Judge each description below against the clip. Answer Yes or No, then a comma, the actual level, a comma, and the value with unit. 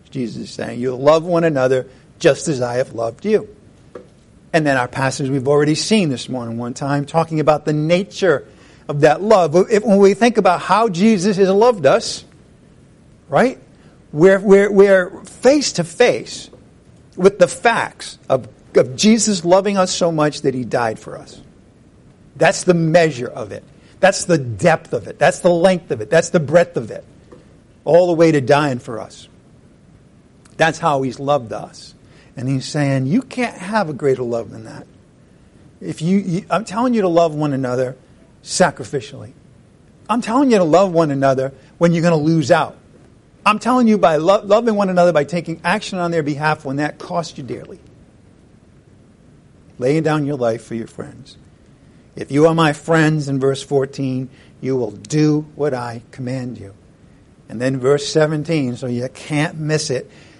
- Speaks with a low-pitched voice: No, medium, 155 Hz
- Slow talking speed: No, average, 175 wpm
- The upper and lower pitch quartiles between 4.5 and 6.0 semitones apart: Yes, average, 5.1 semitones